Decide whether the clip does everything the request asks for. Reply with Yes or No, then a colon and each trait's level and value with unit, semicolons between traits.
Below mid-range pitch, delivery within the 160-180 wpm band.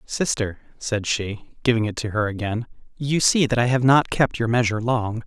No: low, 115 Hz; fast, 205 wpm